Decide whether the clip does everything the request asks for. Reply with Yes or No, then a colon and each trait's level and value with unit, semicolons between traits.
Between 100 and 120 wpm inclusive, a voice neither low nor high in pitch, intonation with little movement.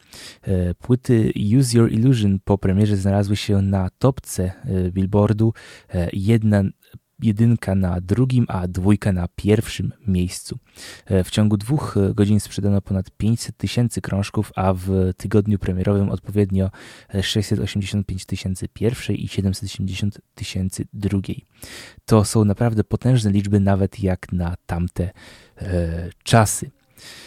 No: average, 115 wpm; low, 100 Hz; narrow, 2.3 semitones